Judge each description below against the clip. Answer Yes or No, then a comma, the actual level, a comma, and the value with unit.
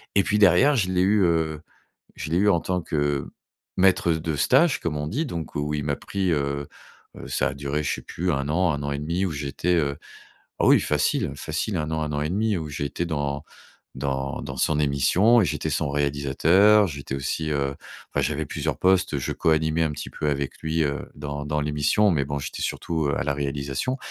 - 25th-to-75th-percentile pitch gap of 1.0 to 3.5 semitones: No, average, 4.0 semitones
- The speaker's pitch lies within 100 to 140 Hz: No, very low, 75 Hz